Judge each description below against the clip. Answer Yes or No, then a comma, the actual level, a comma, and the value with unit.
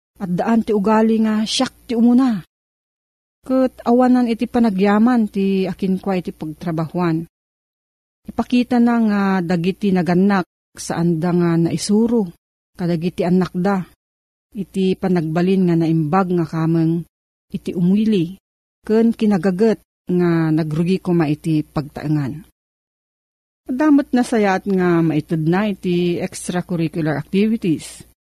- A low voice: No, medium, 185 Hz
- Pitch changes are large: No, average, 4.4 semitones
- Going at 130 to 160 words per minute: No, slow, 110 wpm